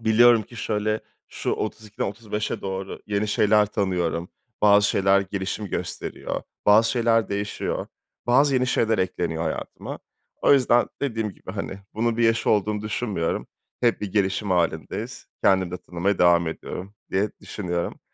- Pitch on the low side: Yes, low, 105 Hz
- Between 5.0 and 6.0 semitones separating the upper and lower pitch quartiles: No, average, 2.9 semitones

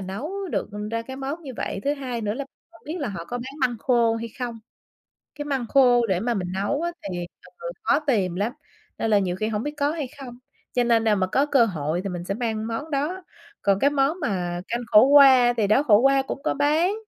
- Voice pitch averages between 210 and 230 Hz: No, high, 240 Hz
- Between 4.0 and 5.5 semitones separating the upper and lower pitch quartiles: Yes, average, 5.1 semitones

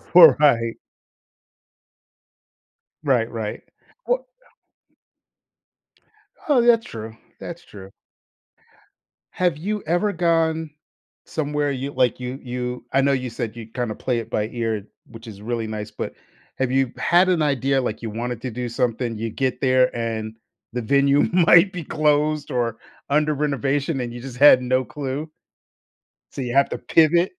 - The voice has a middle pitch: No, low, 130 Hz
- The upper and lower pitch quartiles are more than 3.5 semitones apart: Yes, average, 4.4 semitones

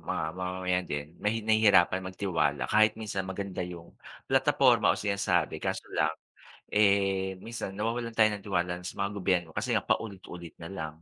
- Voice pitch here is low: Yes, very low, 95 Hz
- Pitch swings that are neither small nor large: Yes, average, 3.2 semitones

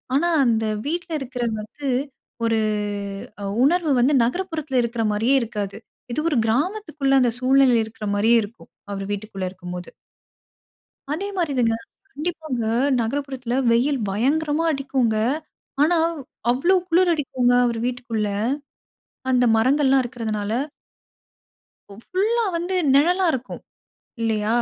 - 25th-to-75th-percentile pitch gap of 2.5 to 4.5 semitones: No, average, 5.2 semitones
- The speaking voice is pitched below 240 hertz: No, very high, 255 Hz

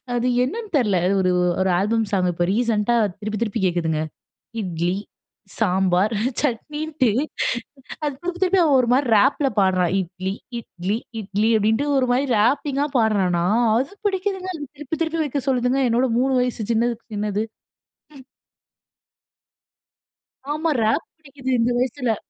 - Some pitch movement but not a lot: No, wide, 5.8 semitones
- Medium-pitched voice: No, high, 235 Hz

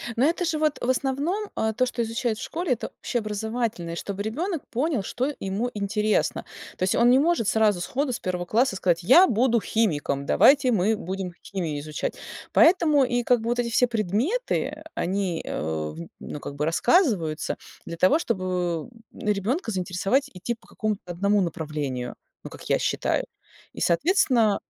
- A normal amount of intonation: No, wide, 6.0 semitones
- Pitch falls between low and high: No, high, 220 Hz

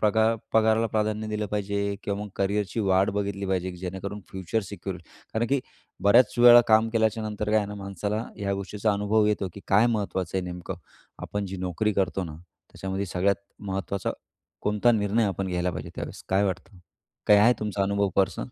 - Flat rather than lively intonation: Yes, narrow, 2.0 semitones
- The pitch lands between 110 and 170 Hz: No, low, 100 Hz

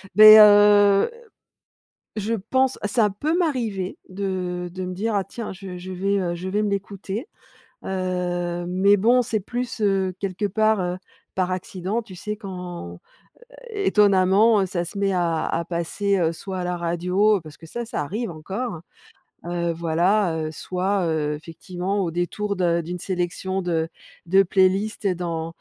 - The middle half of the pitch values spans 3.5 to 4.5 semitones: No, average, 2.8 semitones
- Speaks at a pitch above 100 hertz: Yes, high, 190 Hz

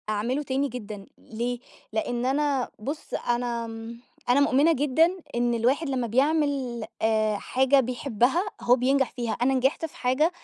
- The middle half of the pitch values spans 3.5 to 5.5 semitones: No, average, 3.0 semitones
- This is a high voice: Yes, very high, 250 Hz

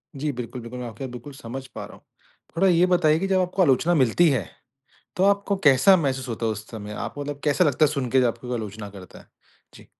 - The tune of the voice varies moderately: No, wide, 6.0 semitones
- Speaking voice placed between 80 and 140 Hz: Yes, low, 135 Hz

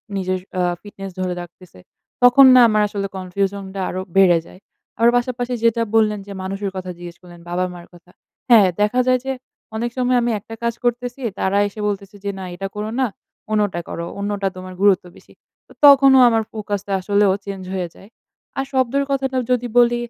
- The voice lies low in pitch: No, high, 205 Hz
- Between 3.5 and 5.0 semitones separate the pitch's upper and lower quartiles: Yes, average, 4.3 semitones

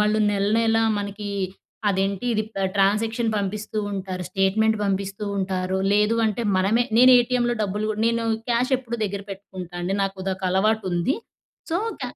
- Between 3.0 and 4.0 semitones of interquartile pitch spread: No, narrow, 2.5 semitones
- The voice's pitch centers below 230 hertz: Yes, high, 205 Hz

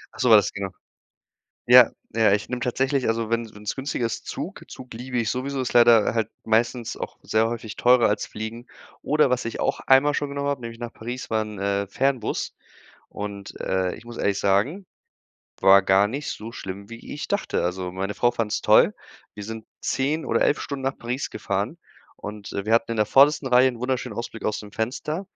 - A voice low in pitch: Yes, low, 115 Hz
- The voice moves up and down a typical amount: Yes, average, 3.5 semitones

